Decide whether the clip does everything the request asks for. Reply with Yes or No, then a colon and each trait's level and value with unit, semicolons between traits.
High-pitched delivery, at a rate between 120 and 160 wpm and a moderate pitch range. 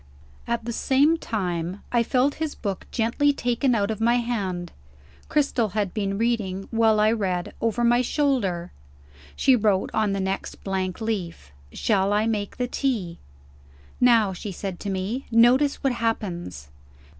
Yes: high, 220 Hz; average, 155 wpm; average, 4.0 semitones